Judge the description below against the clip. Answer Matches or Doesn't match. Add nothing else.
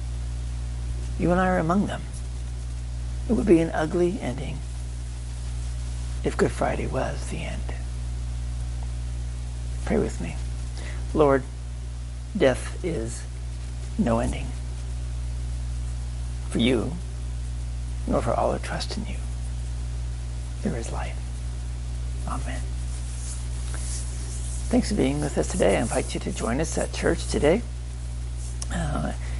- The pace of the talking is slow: Matches